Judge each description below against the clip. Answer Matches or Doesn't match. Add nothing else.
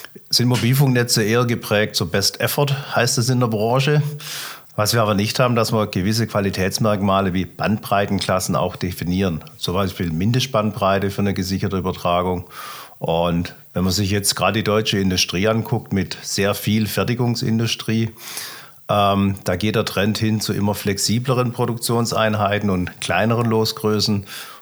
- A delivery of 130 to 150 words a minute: Matches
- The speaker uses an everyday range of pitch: Matches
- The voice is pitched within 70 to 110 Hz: Matches